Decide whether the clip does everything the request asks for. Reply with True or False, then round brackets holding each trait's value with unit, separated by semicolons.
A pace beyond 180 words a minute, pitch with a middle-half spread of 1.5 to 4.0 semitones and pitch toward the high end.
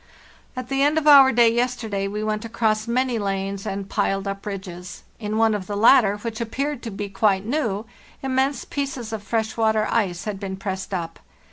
True (195 wpm; 3.4 semitones; 215 Hz)